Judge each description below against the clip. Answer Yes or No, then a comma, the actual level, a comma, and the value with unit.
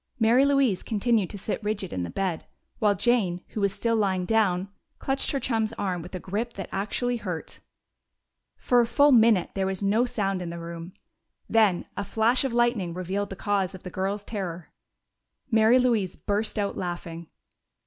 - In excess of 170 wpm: Yes, average, 180 wpm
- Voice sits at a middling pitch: No, high, 205 Hz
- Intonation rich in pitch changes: No, average, 3.7 semitones